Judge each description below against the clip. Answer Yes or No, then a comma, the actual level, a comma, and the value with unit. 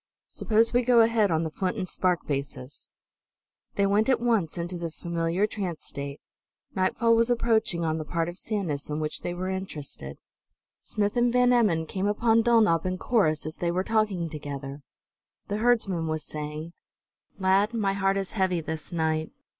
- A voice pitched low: No, medium, 185 Hz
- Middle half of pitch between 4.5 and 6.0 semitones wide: Yes, average, 5.3 semitones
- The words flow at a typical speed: Yes, average, 175 wpm